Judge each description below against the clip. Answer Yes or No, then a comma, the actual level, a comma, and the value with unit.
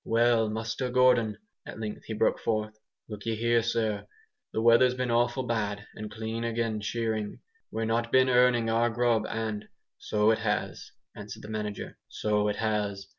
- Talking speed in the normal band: Yes, average, 170 wpm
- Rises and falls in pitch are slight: Yes, narrow, 1.7 semitones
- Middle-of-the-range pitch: No, low, 110 Hz